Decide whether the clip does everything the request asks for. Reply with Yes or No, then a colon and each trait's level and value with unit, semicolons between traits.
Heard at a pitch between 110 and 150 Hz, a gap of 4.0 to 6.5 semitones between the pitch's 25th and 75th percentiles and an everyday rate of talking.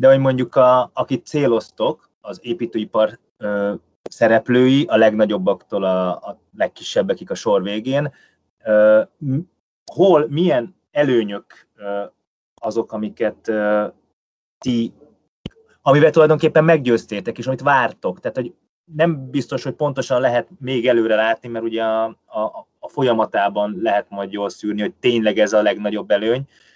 Yes: low, 115 Hz; average, 4.5 semitones; average, 130 wpm